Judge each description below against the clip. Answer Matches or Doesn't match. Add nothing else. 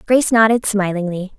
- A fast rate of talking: Doesn't match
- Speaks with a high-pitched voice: Matches